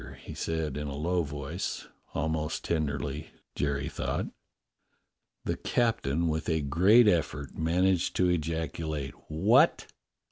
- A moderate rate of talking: No, slow, 120 wpm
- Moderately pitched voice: No, very low, 80 Hz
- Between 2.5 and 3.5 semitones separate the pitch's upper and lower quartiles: Yes, average, 3.1 semitones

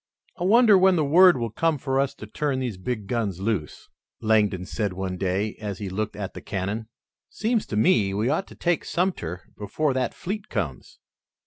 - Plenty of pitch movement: Yes, wide, 7.9 semitones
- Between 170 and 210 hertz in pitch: No, low, 110 Hz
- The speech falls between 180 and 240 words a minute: Yes, average, 195 wpm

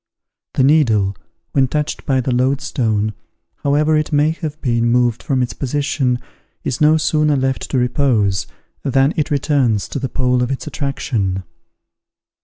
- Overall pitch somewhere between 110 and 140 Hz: Yes, low, 135 Hz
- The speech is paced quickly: No, average, 150 wpm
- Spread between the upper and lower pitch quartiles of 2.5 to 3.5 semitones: Yes, average, 3.2 semitones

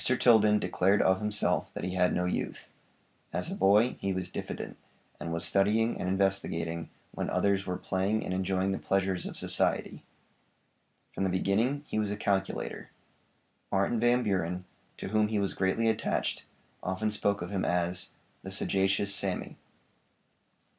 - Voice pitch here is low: Yes, very low, 95 Hz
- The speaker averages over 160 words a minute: No, average, 155 wpm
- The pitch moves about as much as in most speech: No, narrow, 2.2 semitones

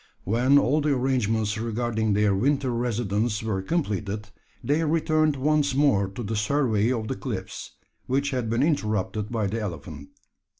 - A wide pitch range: No, average, 4.8 semitones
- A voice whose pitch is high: No, low, 115 Hz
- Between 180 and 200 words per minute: No, average, 155 wpm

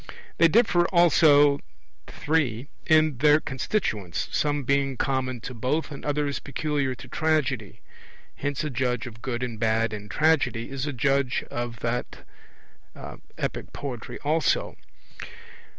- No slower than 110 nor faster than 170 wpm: Yes, slow, 135 wpm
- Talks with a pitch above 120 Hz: Yes, low, 135 Hz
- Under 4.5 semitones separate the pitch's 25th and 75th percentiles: Yes, average, 3.7 semitones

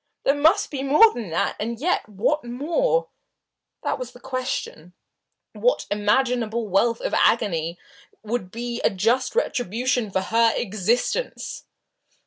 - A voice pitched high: Yes, high, 240 Hz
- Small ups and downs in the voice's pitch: No, average, 4.1 semitones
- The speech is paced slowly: Yes, slow, 130 wpm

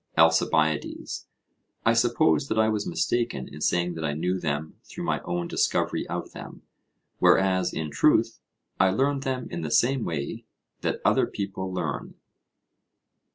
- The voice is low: Yes, very low, 90 Hz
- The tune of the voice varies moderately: No, wide, 6.3 semitones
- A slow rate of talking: No, average, 150 wpm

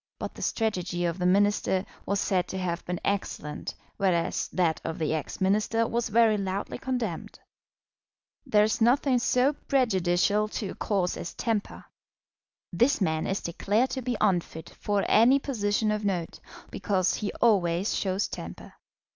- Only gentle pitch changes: No, average, 4.0 semitones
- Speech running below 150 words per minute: No, average, 155 wpm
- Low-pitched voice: No, high, 200 Hz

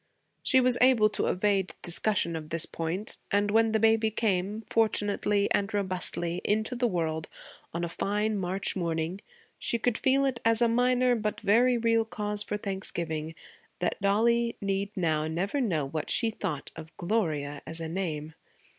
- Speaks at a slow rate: No, average, 165 wpm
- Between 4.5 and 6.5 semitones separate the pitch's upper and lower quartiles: Yes, average, 4.8 semitones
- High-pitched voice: Yes, high, 200 Hz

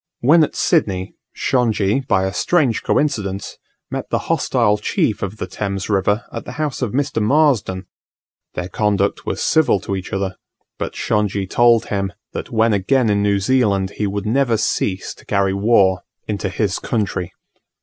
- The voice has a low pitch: Yes, low, 105 Hz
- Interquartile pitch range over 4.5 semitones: No, average, 3.6 semitones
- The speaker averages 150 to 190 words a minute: Yes, average, 165 wpm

